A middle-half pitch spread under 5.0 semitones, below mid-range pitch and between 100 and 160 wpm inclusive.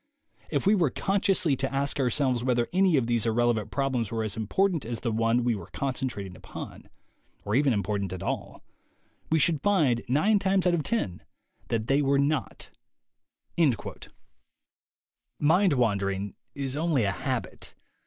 No: wide, 5.5 semitones; low, 130 Hz; average, 155 wpm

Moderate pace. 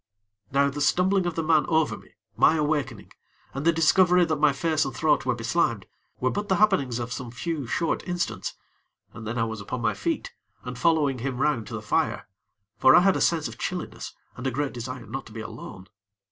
No: fast, 215 wpm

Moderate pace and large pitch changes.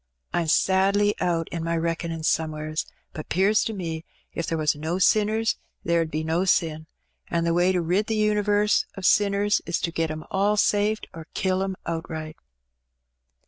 No: average, 180 wpm; average, 3.9 semitones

